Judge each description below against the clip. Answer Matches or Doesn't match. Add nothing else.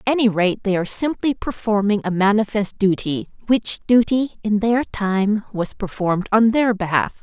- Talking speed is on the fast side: Doesn't match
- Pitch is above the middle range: Matches